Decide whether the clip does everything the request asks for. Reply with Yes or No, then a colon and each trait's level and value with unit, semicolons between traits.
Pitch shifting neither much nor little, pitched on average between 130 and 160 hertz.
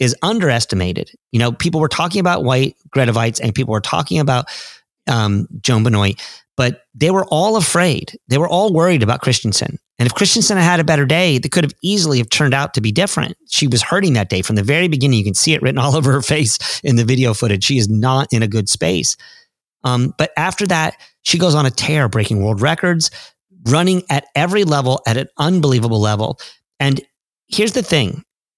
No: wide, 6.6 semitones; medium, 140 Hz